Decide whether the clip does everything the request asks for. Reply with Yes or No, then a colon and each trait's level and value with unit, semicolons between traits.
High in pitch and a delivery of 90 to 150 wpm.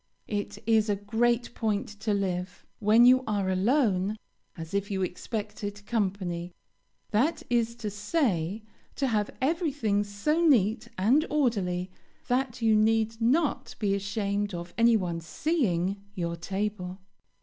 Yes: high, 210 Hz; slow, 135 wpm